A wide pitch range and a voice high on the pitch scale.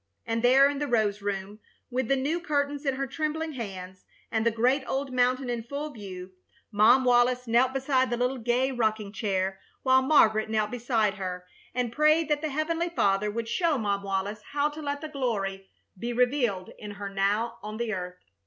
No: average, 4.7 semitones; high, 240 Hz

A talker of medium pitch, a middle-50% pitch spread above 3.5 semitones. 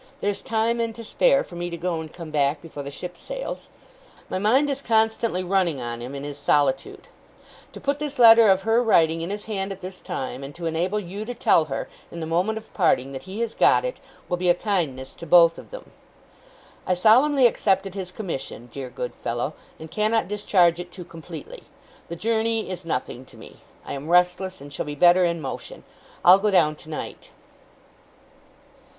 Yes: medium, 180 Hz; wide, 5.5 semitones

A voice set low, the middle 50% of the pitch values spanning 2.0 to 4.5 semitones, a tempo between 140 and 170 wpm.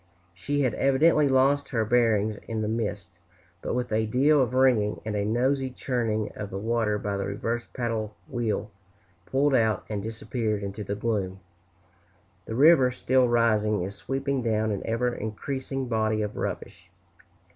Yes: low, 115 Hz; average, 3.5 semitones; average, 160 wpm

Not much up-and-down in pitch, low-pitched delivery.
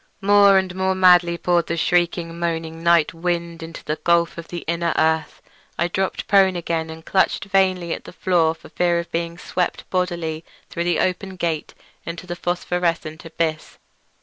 No: narrow, 1.5 semitones; medium, 170 Hz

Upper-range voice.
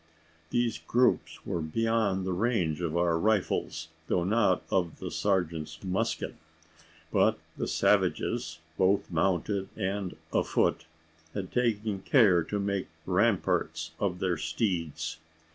No: very low, 95 Hz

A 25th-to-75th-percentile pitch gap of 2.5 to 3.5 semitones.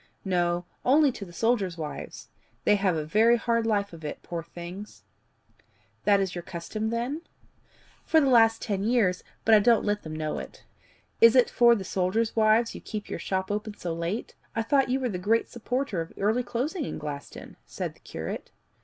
No: average, 4.5 semitones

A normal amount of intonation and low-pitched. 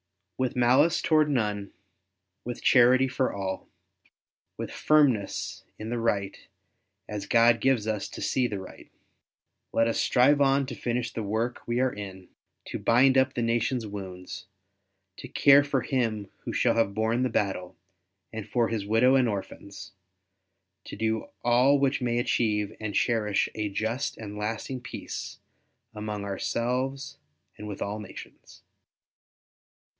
Yes: average, 3.6 semitones; low, 115 Hz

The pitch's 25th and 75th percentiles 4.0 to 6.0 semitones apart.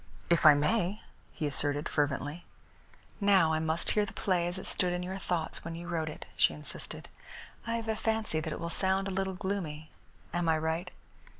No: average, 3.4 semitones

